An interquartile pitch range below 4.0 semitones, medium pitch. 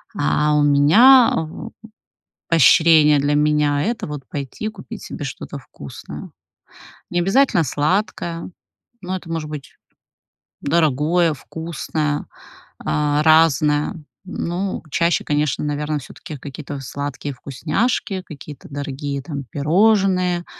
Yes: average, 3.2 semitones; medium, 150 Hz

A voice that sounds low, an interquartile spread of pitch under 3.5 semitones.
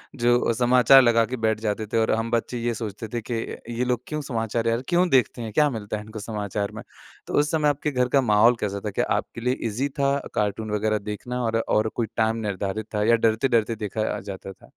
Yes: low, 115 Hz; narrow, 2.6 semitones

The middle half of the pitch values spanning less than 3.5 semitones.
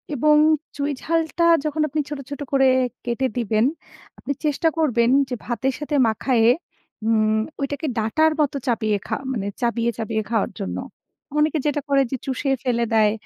No: average, 4.6 semitones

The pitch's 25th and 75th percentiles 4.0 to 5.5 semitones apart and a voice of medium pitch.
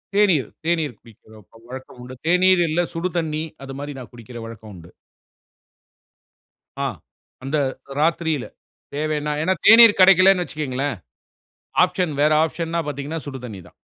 Yes: average, 4.9 semitones; medium, 150 Hz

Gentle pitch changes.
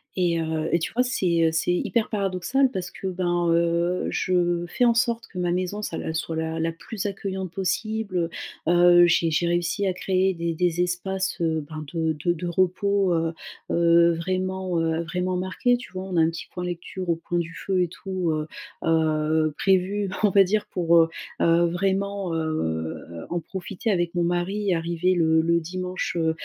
Yes: narrow, 2.2 semitones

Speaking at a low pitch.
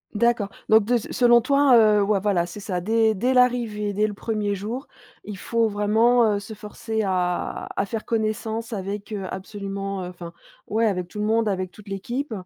No: high, 210 Hz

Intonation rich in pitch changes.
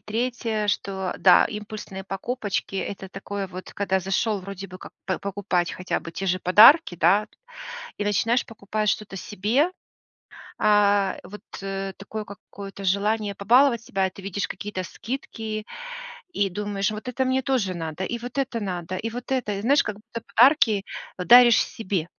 No: average, 2.9 semitones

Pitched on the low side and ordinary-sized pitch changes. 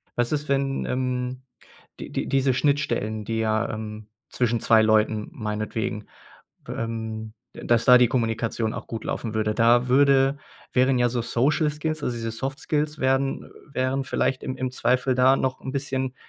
Yes: low, 125 Hz; average, 3.2 semitones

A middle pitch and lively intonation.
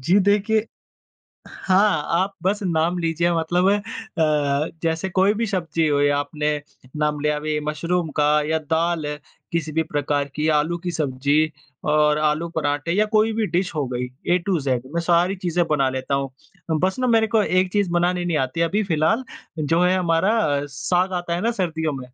No: medium, 165 Hz; average, 3.6 semitones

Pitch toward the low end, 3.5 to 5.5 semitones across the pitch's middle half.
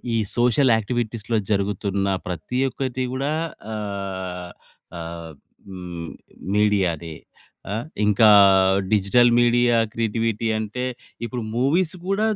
Yes: low, 105 Hz; average, 4.2 semitones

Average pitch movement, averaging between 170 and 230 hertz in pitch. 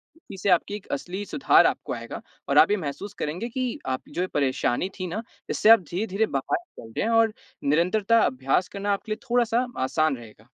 No: wide, 7.6 semitones; high, 190 Hz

